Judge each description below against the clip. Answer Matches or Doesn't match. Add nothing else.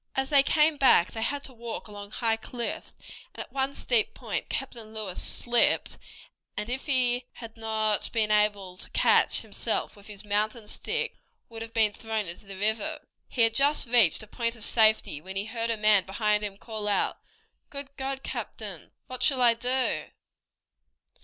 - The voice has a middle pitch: Doesn't match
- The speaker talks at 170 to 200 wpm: Matches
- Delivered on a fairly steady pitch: Doesn't match